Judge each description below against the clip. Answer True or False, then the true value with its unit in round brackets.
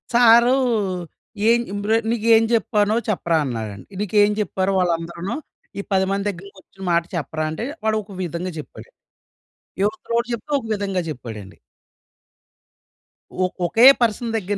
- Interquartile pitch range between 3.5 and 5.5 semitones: True (4.5 semitones)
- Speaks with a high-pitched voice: True (200 Hz)